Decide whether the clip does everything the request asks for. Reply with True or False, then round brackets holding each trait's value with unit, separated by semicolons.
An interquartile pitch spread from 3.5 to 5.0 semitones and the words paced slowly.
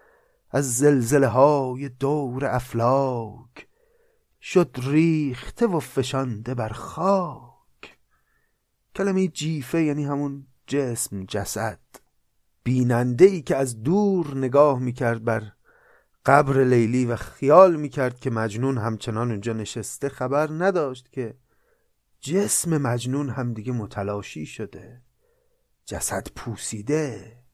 True (4.3 semitones; 100 wpm)